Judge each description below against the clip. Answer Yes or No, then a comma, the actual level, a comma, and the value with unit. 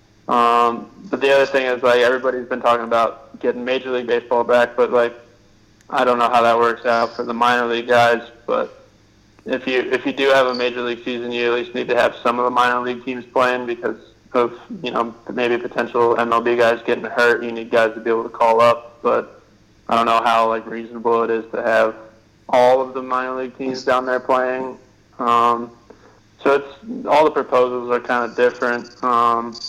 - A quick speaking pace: Yes, fast, 210 wpm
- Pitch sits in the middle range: No, low, 120 Hz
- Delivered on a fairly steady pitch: Yes, narrow, 1.3 semitones